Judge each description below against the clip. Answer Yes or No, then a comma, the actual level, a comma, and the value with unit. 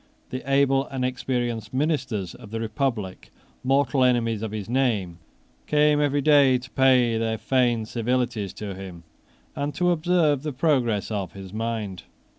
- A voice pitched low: Yes, low, 125 Hz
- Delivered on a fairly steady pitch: No, average, 3.9 semitones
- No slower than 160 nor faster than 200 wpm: No, average, 150 wpm